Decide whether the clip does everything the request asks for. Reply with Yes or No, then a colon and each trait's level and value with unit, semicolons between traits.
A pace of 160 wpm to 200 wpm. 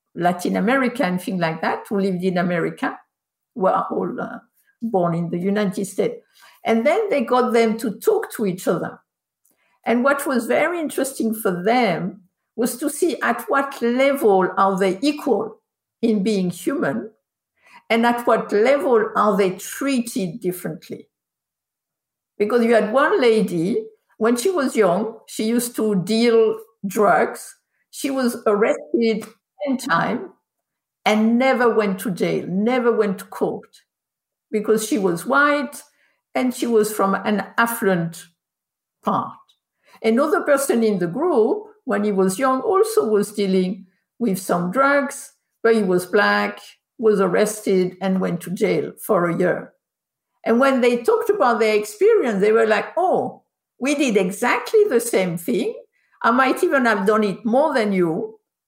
No: average, 150 wpm